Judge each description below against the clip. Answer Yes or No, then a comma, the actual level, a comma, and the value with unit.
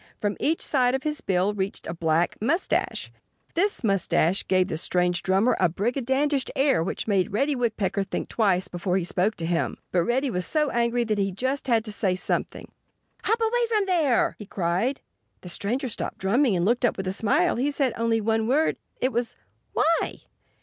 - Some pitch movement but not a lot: No, wide, 6.1 semitones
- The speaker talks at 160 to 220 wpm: Yes, average, 190 wpm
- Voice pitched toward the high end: Yes, high, 225 Hz